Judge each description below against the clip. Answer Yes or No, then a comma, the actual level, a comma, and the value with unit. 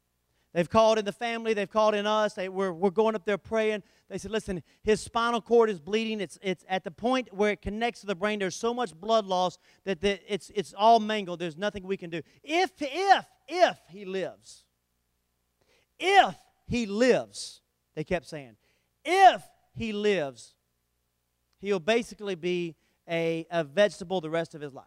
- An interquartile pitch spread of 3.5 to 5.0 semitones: Yes, average, 4.6 semitones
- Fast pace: No, average, 185 wpm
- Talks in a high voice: Yes, high, 200 Hz